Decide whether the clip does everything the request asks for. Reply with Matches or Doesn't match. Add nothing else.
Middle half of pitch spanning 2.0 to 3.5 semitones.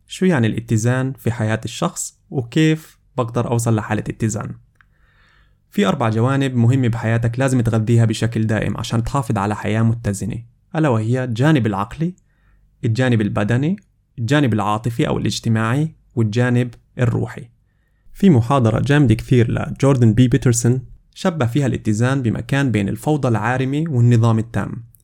Matches